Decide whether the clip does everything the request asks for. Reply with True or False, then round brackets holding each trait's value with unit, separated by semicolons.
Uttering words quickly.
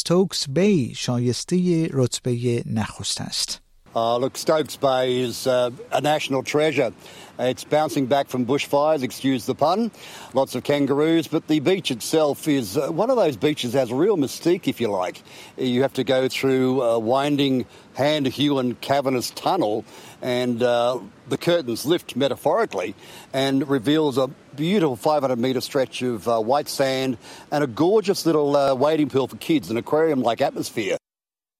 True (160 wpm)